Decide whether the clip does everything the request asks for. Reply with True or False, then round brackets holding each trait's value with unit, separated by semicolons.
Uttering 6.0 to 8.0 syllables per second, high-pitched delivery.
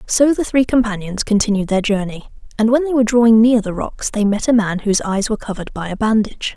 True (6.4 syllables/s; 220 Hz)